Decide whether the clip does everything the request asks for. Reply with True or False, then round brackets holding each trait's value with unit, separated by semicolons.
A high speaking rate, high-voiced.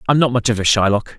False (305 wpm; 115 Hz)